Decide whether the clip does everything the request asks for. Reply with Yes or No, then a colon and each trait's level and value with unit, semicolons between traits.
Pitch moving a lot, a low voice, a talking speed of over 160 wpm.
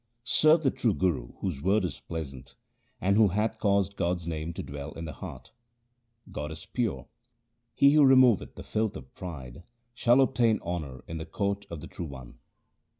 Yes: wide, 6.5 semitones; very low, 90 Hz; average, 180 wpm